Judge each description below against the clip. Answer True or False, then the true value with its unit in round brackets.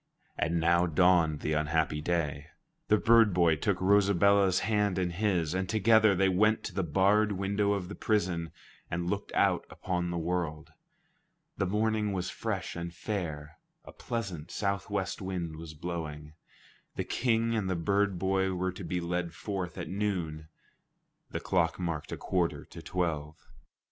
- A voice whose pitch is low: True (90 Hz)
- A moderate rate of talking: True (160 wpm)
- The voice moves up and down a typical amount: True (3.3 semitones)